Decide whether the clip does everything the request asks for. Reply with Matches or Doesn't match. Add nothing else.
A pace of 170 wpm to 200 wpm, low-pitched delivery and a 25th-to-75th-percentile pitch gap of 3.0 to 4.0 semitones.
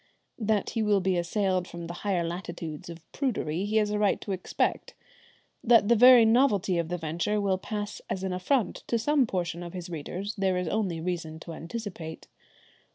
Doesn't match